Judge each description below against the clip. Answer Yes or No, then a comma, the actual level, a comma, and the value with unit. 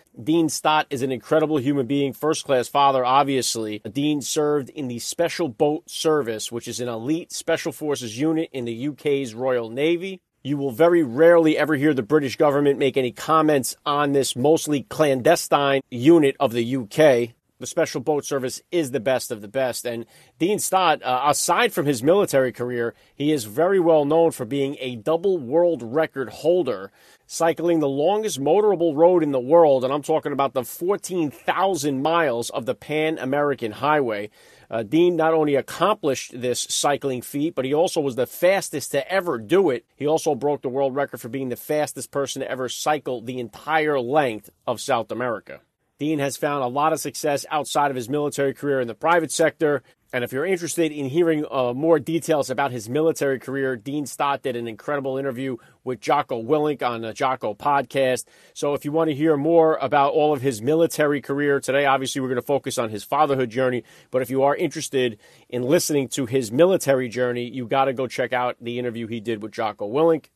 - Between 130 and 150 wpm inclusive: No, average, 195 wpm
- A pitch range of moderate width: Yes, average, 3.4 semitones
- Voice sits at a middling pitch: Yes, medium, 145 Hz